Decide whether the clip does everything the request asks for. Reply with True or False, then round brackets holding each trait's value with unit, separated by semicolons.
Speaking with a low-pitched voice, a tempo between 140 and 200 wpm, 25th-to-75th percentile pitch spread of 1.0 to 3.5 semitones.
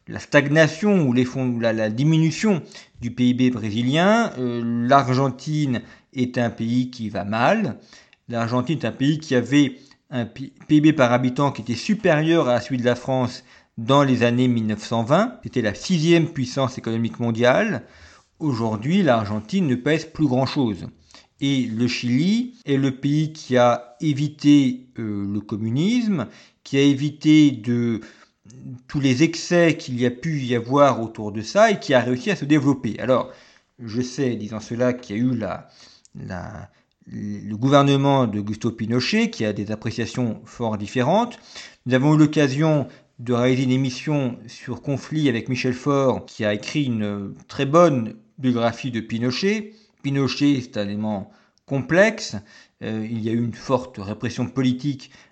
False (125 Hz; 160 wpm; 4.0 semitones)